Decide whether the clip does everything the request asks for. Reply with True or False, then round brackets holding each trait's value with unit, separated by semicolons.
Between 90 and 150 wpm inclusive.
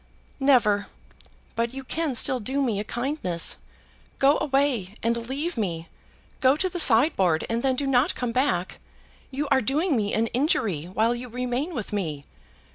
False (165 wpm)